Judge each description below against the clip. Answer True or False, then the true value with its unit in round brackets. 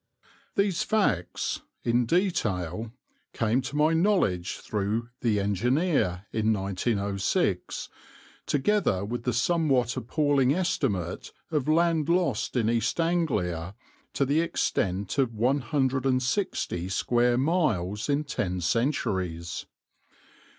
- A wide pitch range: True (7.2 semitones)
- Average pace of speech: False (100 wpm)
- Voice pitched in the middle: False (120 Hz)